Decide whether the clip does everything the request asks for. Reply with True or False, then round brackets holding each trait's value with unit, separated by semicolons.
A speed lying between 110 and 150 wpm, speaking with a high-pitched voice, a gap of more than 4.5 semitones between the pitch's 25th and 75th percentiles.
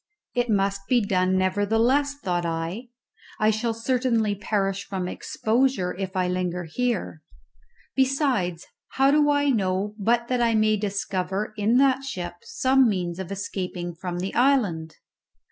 True (145 wpm; 205 Hz; 5.2 semitones)